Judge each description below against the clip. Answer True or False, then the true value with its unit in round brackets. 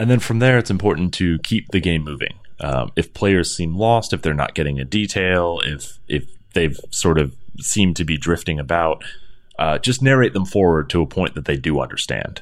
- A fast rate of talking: True (215 wpm)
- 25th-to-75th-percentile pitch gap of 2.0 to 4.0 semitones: False (4.7 semitones)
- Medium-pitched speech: False (85 Hz)